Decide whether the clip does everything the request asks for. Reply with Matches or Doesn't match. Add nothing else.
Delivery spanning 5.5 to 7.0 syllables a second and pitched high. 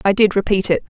Matches